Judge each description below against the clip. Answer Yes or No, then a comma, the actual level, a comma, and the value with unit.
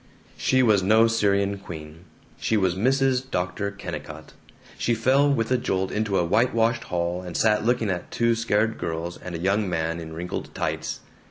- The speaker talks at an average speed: Yes, average, 175 wpm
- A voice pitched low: Yes, low, 100 Hz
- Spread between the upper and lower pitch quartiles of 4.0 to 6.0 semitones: Yes, average, 4.6 semitones